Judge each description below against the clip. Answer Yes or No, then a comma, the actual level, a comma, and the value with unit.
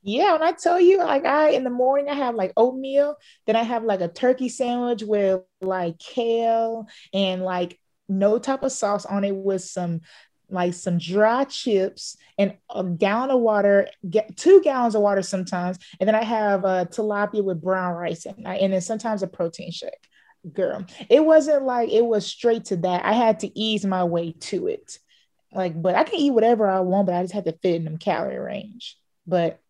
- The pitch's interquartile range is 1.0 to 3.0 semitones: No, average, 4.6 semitones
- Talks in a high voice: Yes, high, 205 Hz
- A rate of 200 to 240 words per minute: Yes, fast, 205 wpm